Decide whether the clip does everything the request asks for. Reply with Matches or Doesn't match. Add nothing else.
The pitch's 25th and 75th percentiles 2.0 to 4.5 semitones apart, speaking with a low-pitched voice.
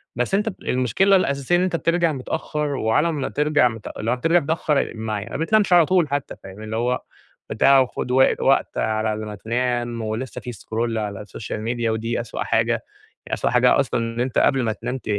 Doesn't match